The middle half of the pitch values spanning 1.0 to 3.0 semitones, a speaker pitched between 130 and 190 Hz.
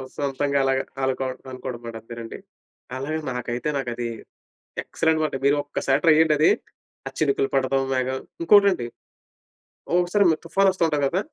No: average, 3.7 semitones; medium, 140 Hz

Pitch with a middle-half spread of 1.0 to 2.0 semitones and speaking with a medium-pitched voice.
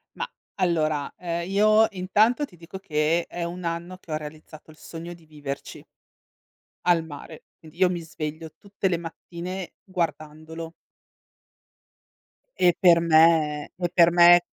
No: narrow, 2.4 semitones; medium, 170 Hz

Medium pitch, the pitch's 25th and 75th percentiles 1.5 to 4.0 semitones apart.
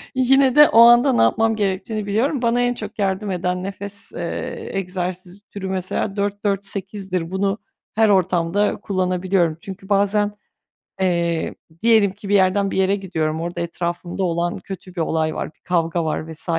No: high, 195 Hz; average, 2.7 semitones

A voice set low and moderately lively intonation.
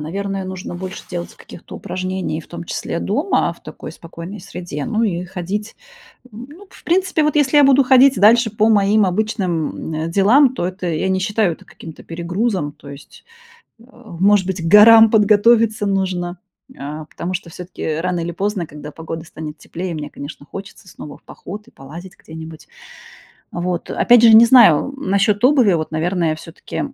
No: medium, 185 Hz; average, 4.6 semitones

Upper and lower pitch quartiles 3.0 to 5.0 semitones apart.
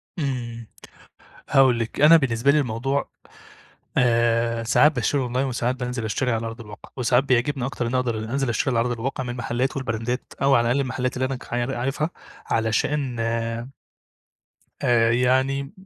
No: narrow, 2.5 semitones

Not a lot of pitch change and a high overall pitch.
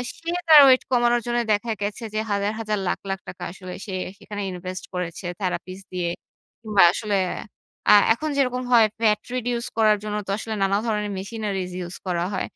No: average, 3.8 semitones; high, 210 Hz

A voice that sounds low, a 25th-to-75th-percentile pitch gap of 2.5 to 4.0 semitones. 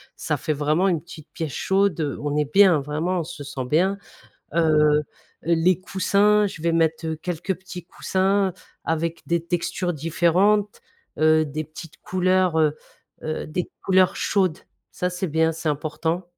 No: medium, 165 Hz; average, 3.0 semitones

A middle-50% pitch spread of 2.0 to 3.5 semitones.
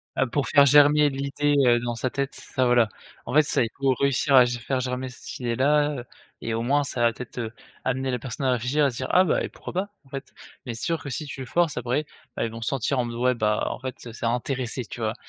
Yes: average, 2.7 semitones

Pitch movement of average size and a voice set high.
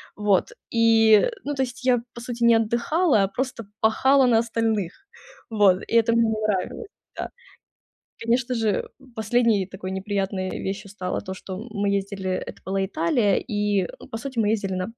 Yes: average, 3.2 semitones; high, 215 Hz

